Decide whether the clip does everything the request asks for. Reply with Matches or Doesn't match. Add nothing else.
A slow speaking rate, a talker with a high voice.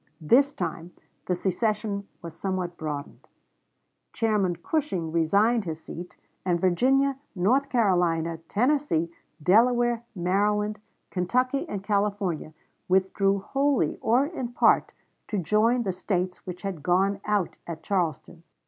Matches